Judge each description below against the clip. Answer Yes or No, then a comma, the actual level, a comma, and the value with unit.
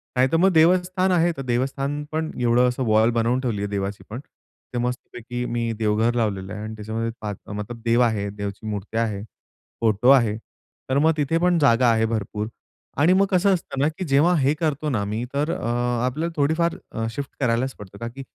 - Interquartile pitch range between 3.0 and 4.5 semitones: No, average, 5.1 semitones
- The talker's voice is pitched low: Yes, low, 125 Hz